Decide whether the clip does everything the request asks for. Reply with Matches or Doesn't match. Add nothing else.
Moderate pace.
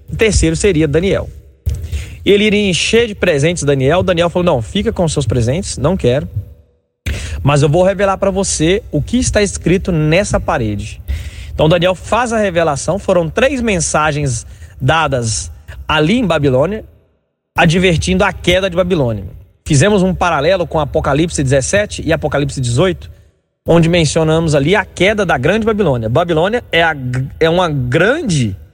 Matches